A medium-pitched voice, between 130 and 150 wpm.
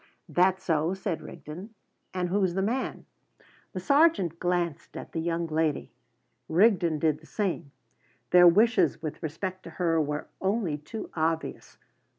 Yes: medium, 175 Hz; average, 145 wpm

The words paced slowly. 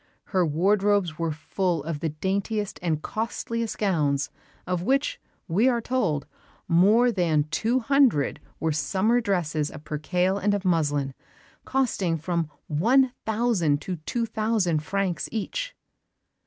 Yes: slow, 130 wpm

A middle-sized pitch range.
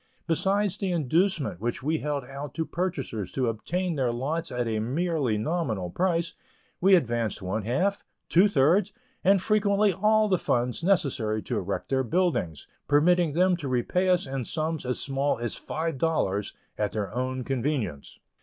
No: wide, 6.9 semitones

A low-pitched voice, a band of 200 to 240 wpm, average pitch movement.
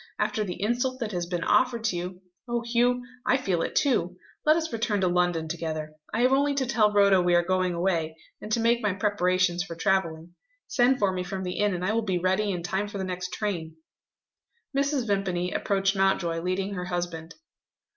No: high, 190 Hz; fast, 205 wpm; average, 4.1 semitones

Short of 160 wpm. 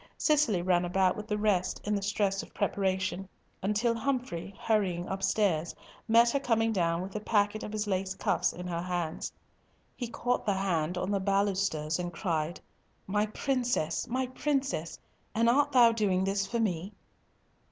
No: average, 165 wpm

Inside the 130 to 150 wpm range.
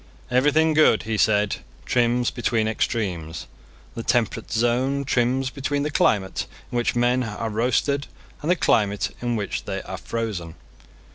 Yes: average, 145 wpm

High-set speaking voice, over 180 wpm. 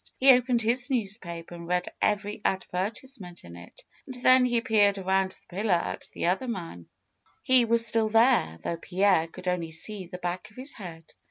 Yes: high, 200 Hz; average, 195 wpm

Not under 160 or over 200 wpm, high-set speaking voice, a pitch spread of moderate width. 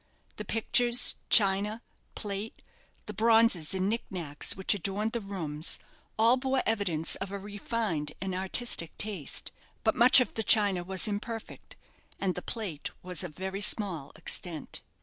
No: average, 150 wpm; high, 200 Hz; average, 3.7 semitones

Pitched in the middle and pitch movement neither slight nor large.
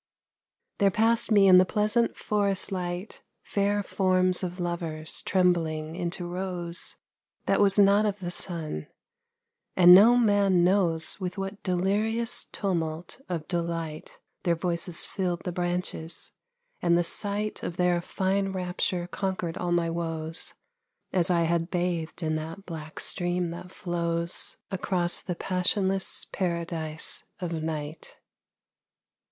No: medium, 180 Hz; narrow, 2.3 semitones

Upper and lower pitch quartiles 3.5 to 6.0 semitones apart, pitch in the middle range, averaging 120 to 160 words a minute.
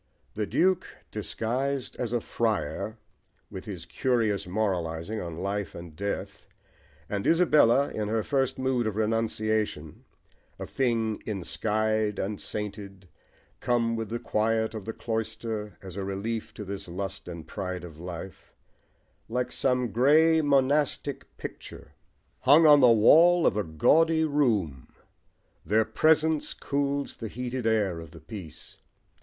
No: average, 4.7 semitones; low, 110 Hz; slow, 135 wpm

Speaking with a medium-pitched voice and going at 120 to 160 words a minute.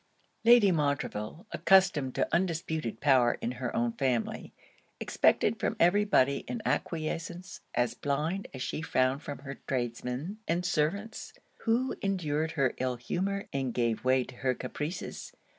Yes: medium, 150 Hz; average, 140 wpm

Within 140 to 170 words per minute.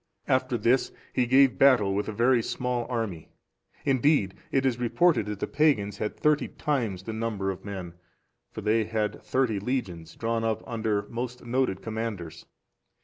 Yes: average, 160 wpm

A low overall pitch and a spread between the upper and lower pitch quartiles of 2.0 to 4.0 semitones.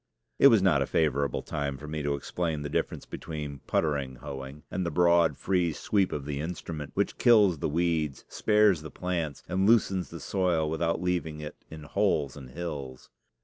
Yes: very low, 80 Hz; average, 3.7 semitones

